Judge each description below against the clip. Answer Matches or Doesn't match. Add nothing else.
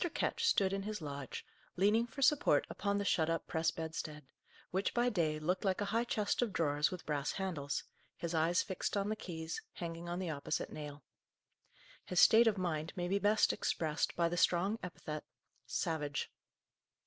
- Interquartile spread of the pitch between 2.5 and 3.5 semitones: Doesn't match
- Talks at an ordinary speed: Matches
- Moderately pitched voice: Matches